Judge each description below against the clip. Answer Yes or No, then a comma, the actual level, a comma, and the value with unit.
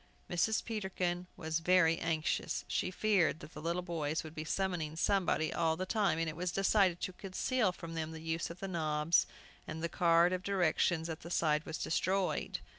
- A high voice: No, medium, 170 Hz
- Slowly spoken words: No, average, 190 wpm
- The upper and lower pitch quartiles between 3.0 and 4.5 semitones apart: No, narrow, 2.5 semitones